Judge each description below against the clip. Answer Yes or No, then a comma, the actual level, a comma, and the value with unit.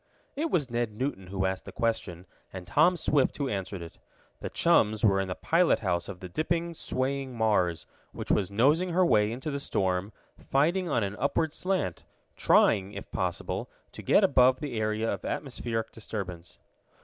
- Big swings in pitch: Yes, wide, 6.8 semitones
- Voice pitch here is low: Yes, low, 115 Hz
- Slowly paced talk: No, average, 175 wpm